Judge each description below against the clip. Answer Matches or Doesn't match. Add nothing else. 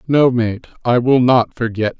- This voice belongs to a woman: Doesn't match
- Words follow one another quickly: Doesn't match